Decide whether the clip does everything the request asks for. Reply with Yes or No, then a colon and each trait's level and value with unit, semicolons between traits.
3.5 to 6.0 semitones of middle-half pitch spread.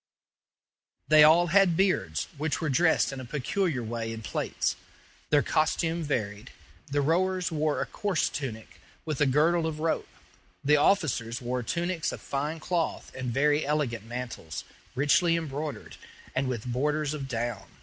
Yes: average, 4.5 semitones